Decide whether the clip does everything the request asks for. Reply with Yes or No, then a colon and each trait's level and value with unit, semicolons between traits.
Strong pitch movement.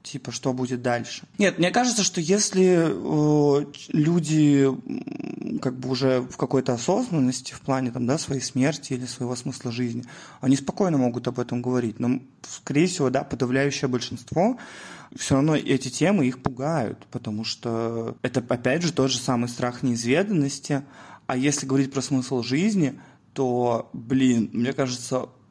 No: average, 3.2 semitones